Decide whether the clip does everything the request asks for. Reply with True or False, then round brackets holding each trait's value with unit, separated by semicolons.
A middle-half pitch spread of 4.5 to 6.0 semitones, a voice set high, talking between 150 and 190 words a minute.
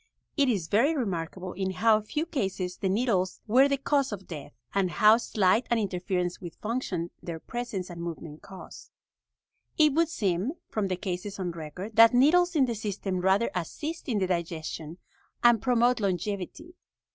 True (5.2 semitones; 200 Hz; 170 wpm)